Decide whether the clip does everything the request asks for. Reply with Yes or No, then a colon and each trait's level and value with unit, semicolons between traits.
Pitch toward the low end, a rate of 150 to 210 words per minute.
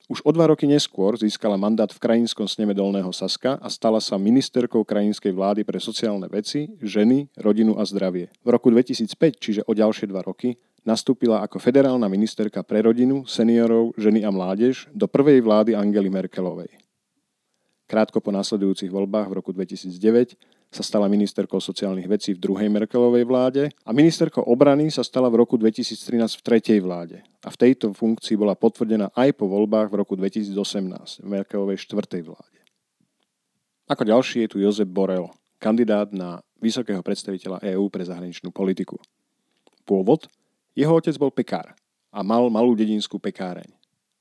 Yes: low, 110 Hz; average, 155 wpm